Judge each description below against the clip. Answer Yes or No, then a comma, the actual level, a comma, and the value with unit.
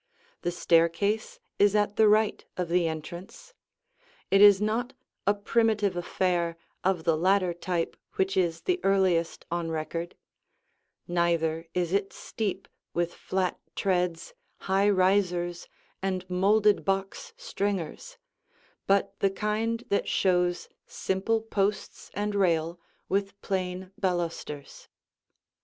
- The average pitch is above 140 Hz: Yes, high, 190 Hz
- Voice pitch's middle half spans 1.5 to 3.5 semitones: Yes, average, 2.8 semitones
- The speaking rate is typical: No, slow, 115 wpm